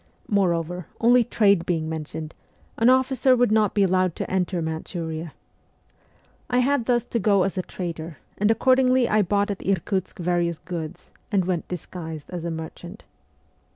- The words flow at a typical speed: Yes, average, 155 wpm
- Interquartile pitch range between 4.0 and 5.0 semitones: Yes, average, 4.5 semitones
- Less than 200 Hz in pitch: Yes, medium, 185 Hz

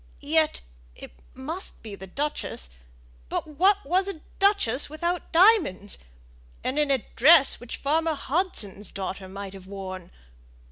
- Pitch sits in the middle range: No, very high, 280 Hz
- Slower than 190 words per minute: Yes, slow, 135 wpm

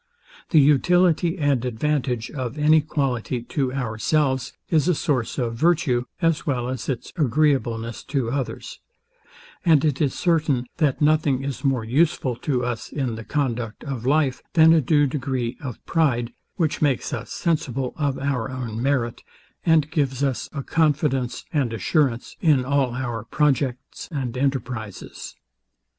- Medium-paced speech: Yes, average, 150 wpm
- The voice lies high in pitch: No, low, 135 Hz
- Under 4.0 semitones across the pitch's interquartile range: Yes, average, 3.5 semitones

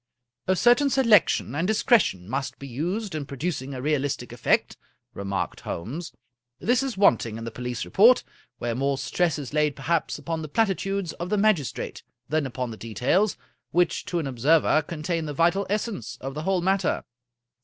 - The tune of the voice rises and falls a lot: Yes, wide, 6.9 semitones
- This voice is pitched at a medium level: Yes, medium, 155 Hz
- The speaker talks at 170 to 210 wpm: Yes, average, 185 wpm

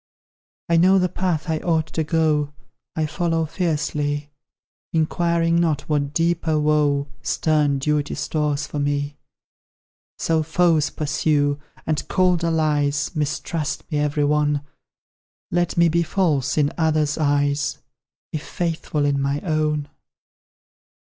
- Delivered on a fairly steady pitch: Yes, narrow, 2.1 semitones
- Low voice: No, medium, 155 Hz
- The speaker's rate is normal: No, slow, 120 wpm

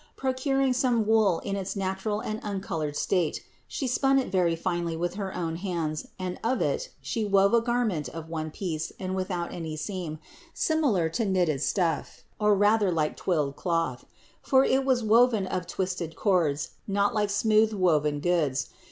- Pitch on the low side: No, high, 190 Hz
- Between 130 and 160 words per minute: No, average, 170 wpm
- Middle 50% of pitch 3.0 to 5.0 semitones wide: Yes, average, 4.7 semitones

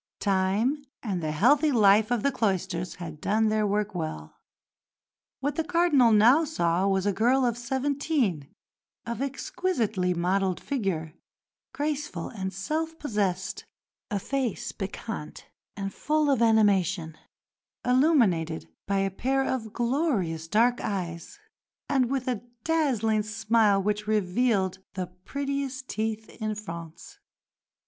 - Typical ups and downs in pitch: No, wide, 5.7 semitones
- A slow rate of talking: Yes, slow, 125 wpm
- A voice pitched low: No, high, 215 Hz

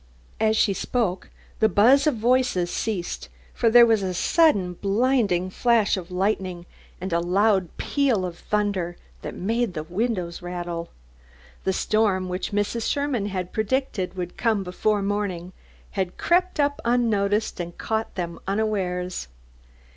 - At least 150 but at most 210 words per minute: No, average, 140 wpm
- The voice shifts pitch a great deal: No, average, 3.9 semitones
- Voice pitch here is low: No, high, 200 Hz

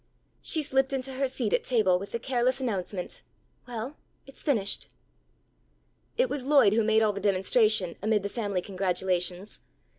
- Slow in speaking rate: No, average, 155 wpm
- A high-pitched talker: Yes, high, 220 Hz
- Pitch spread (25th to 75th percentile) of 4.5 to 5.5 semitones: Yes, average, 5.0 semitones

